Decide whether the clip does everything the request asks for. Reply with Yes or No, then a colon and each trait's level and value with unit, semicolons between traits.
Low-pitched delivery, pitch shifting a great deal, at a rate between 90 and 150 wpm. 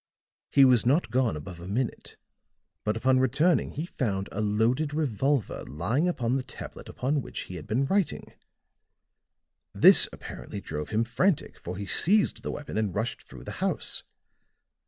No: low, 120 Hz; wide, 5.7 semitones; average, 160 wpm